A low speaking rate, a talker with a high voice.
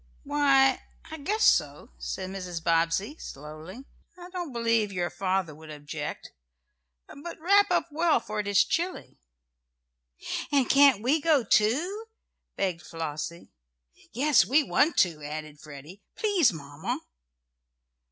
Yes: slow, 125 wpm; high, 210 Hz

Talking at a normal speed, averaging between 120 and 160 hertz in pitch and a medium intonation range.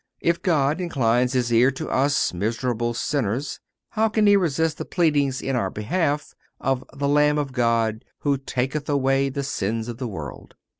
Yes: average, 170 wpm; low, 135 Hz; average, 3.8 semitones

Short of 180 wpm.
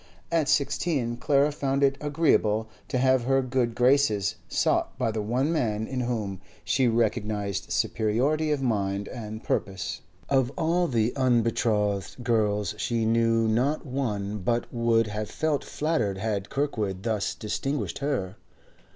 Yes: average, 140 wpm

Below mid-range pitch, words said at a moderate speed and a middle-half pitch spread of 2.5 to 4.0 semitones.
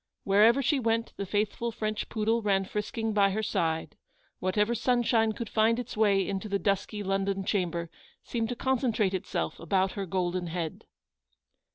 No: high, 210 Hz; average, 165 wpm; average, 2.8 semitones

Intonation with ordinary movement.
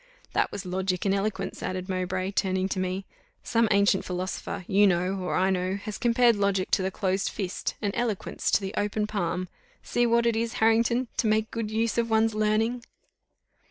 Yes: average, 3.0 semitones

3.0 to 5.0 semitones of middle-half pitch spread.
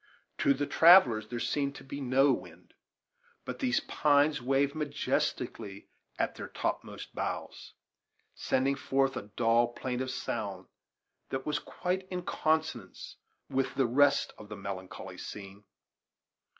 Yes: average, 3.6 semitones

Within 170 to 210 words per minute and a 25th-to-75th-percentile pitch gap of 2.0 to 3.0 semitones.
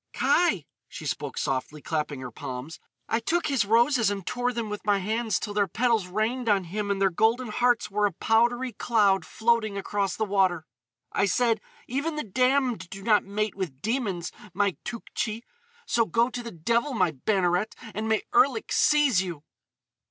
No: average, 175 wpm; average, 3.7 semitones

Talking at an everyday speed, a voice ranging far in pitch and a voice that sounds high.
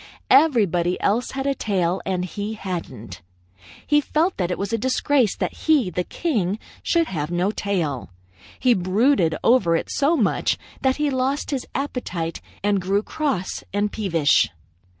Yes: average, 155 wpm; wide, 6.9 semitones; high, 205 Hz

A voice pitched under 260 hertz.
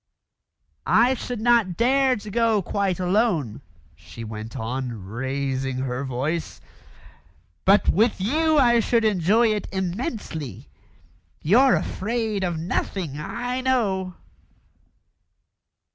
Yes: high, 190 Hz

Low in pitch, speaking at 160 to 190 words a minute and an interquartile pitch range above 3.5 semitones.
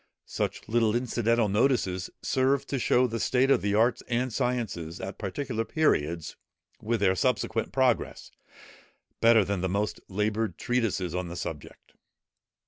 No: low, 110 Hz; average, 140 wpm; average, 4.5 semitones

